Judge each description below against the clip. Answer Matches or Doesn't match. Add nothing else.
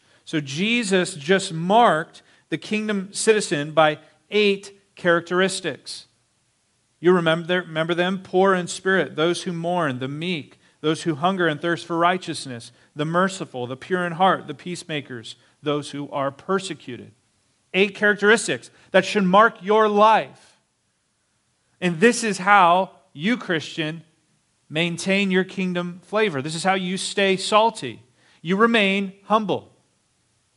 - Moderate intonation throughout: Matches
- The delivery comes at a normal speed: Doesn't match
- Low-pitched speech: Doesn't match